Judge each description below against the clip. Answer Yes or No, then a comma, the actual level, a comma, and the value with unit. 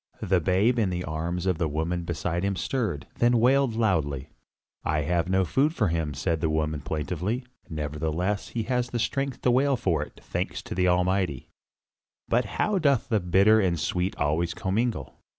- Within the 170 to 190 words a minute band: Yes, average, 185 wpm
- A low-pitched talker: Yes, very low, 90 Hz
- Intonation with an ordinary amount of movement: No, wide, 5.9 semitones